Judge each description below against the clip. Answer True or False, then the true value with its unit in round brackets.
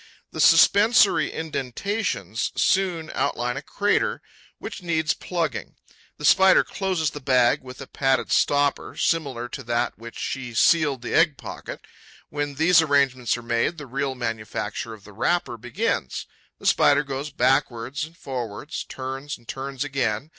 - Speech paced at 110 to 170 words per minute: True (150 wpm)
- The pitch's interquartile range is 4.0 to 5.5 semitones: True (4.6 semitones)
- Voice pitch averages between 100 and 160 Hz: True (135 Hz)